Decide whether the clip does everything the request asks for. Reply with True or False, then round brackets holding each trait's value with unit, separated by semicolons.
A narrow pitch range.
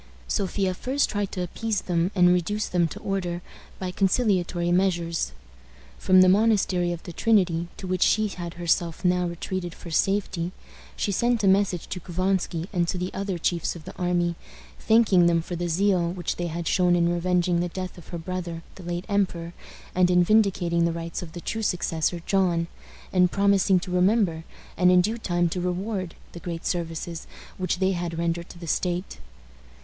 True (1.9 semitones)